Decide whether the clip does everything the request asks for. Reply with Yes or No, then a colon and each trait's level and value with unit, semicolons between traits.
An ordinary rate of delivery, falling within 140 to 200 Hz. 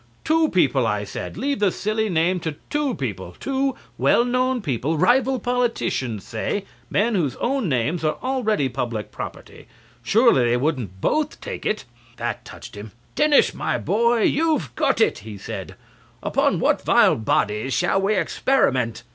Yes: average, 160 wpm; medium, 185 Hz